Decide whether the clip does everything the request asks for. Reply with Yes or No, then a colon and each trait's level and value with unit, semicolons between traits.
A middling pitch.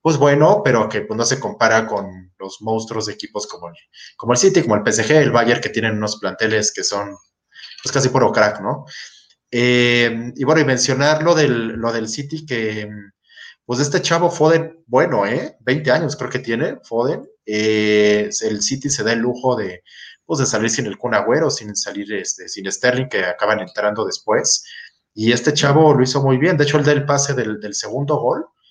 No: low, 120 Hz